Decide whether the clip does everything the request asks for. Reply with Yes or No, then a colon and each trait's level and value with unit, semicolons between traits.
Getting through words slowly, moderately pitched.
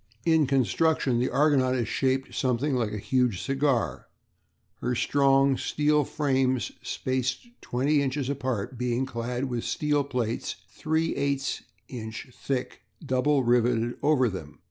No: slow, 125 wpm; low, 130 Hz